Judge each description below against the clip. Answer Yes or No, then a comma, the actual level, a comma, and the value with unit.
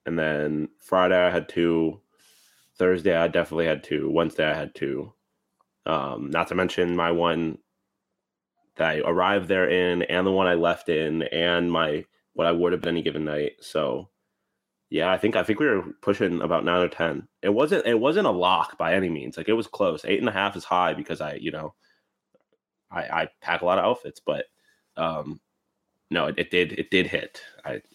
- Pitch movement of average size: No, narrow, 1.6 semitones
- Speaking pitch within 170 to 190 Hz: No, very low, 85 Hz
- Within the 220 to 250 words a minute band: No, fast, 205 wpm